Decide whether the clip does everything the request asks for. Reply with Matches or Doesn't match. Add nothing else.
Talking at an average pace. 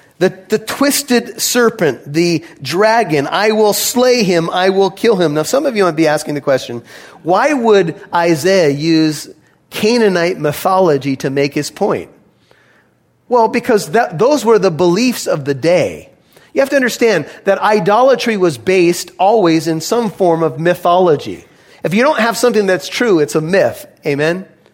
Matches